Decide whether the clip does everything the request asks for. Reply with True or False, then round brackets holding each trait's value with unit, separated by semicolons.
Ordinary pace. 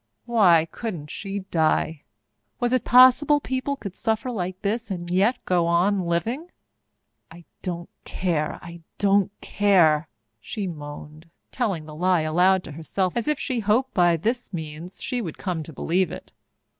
True (160 wpm)